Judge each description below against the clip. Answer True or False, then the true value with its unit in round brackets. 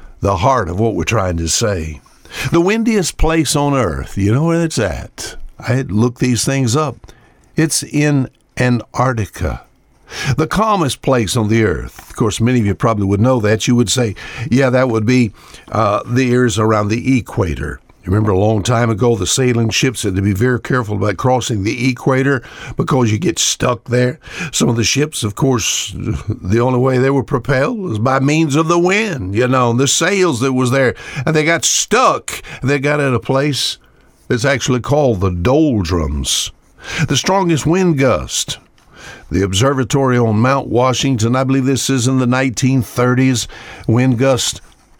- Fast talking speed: False (180 wpm)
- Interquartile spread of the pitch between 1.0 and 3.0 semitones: False (3.6 semitones)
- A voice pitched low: True (125 Hz)